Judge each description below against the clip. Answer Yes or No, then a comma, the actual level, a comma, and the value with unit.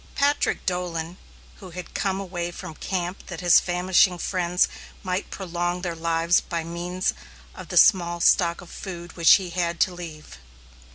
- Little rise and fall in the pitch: Yes, narrow, 1.2 semitones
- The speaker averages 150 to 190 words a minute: Yes, average, 160 wpm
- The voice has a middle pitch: Yes, medium, 175 Hz